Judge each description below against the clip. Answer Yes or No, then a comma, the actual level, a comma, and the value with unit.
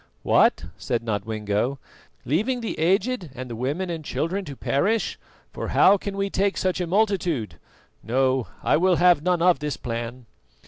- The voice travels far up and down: Yes, wide, 7.2 semitones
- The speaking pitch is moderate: Yes, medium, 165 Hz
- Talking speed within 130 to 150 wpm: No, average, 165 wpm